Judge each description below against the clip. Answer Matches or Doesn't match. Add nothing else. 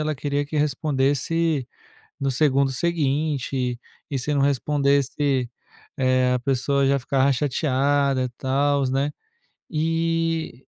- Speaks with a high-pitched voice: Doesn't match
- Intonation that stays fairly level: Matches